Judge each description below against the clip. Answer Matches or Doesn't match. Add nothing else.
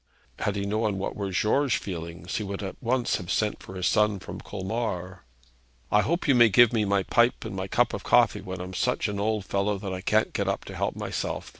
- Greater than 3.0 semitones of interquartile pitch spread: Doesn't match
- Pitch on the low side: Matches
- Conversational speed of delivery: Doesn't match